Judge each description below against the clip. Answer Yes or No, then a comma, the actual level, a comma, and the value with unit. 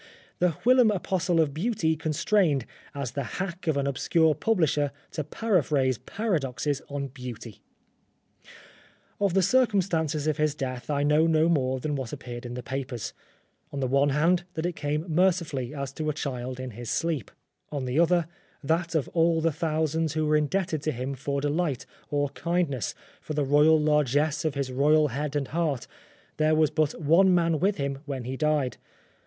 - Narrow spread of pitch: No, average, 3.2 semitones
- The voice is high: No, medium, 150 Hz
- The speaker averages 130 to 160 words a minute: No, average, 180 wpm